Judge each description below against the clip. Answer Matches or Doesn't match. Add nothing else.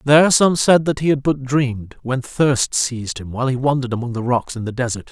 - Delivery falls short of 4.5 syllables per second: Doesn't match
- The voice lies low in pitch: Matches